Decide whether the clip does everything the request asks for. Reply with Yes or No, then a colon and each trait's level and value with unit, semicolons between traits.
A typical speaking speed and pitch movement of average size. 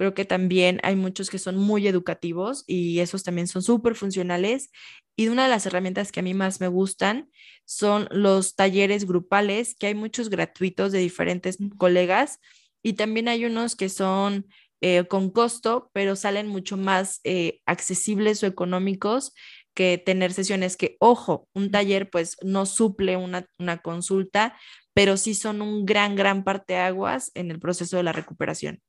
No: average, 170 wpm; narrow, 2.3 semitones